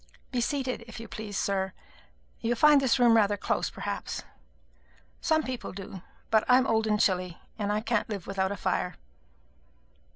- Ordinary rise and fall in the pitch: Yes, average, 3.6 semitones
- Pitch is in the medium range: No, high, 220 Hz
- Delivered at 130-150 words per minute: No, average, 165 wpm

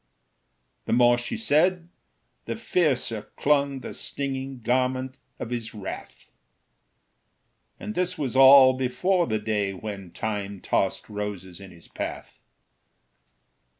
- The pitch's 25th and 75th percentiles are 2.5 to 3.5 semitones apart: No, average, 5.2 semitones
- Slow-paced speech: Yes, slow, 115 wpm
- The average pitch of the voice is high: No, low, 125 Hz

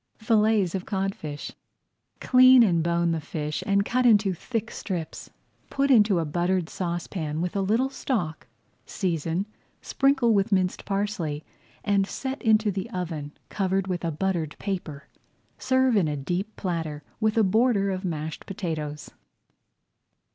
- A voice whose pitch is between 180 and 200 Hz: Yes, high, 190 Hz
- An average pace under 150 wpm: Yes, average, 140 wpm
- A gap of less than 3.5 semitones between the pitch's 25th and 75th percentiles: No, average, 4.6 semitones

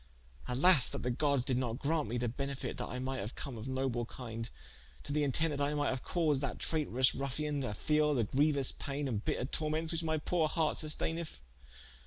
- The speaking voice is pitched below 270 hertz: Yes, medium, 140 Hz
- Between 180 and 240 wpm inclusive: Yes, fast, 205 wpm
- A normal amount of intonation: Yes, average, 3.3 semitones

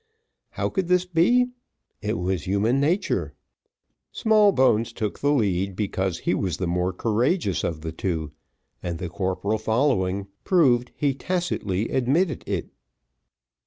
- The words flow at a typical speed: No, slow, 130 wpm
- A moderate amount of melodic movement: No, wide, 8.1 semitones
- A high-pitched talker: No, low, 110 Hz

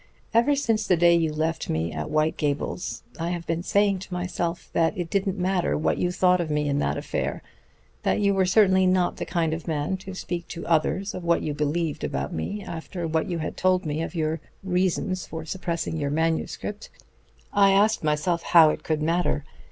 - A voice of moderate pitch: Yes, medium, 170 Hz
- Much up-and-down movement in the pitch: No, average, 2.9 semitones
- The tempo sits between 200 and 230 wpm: Yes, fast, 205 wpm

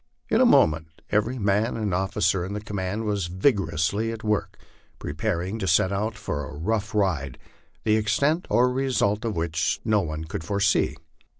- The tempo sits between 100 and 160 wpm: No, average, 170 wpm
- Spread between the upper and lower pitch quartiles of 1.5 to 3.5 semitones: No, average, 4.2 semitones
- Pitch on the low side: Yes, low, 100 Hz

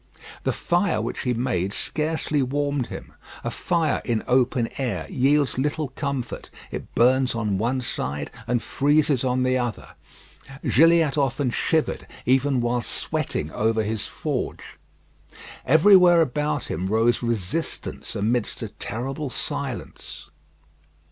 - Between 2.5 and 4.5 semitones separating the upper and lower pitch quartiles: Yes, average, 3.9 semitones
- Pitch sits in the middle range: No, low, 130 Hz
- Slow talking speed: Yes, slow, 125 wpm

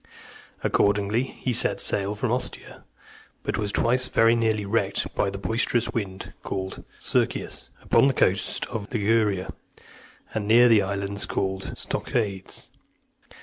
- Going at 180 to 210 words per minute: No, slow, 135 wpm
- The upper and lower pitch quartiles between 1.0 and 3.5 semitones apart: Yes, average, 2.7 semitones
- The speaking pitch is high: No, low, 105 Hz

